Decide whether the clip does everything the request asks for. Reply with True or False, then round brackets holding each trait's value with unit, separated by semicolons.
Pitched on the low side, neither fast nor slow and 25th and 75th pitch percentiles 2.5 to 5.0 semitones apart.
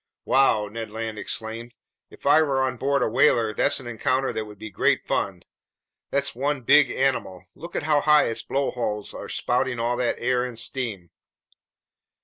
True (125 Hz; 170 wpm; 3.4 semitones)